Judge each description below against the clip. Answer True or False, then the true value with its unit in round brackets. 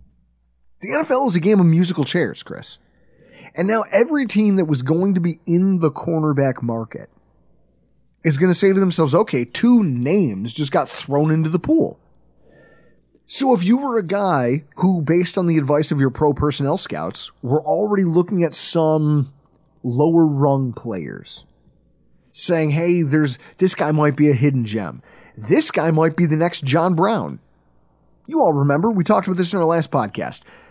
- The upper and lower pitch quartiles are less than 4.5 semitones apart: False (4.9 semitones)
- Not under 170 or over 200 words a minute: True (175 wpm)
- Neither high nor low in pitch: True (160 Hz)